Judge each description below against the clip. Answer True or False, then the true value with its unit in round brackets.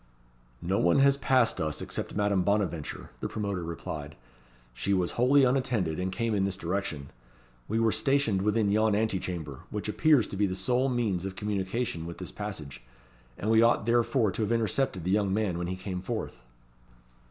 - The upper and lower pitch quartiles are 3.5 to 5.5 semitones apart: True (3.9 semitones)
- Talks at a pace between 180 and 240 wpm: True (185 wpm)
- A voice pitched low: True (100 Hz)